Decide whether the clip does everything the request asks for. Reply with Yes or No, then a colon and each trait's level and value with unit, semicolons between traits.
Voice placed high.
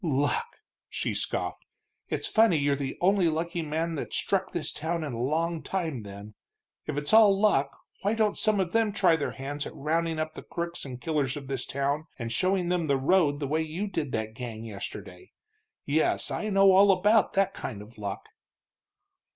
No: medium, 160 Hz